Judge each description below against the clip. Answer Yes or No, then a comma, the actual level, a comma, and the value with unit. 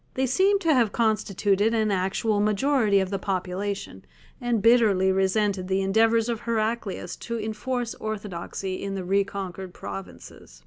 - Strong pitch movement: No, average, 3.0 semitones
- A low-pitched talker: No, high, 205 Hz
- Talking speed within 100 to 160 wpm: Yes, average, 140 wpm